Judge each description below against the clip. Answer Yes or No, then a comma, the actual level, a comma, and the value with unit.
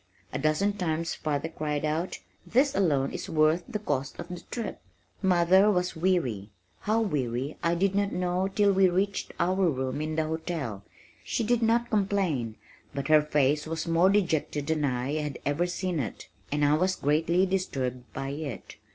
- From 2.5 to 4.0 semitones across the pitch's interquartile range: No, average, 4.5 semitones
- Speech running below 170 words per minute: No, average, 175 wpm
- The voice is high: No, medium, 165 Hz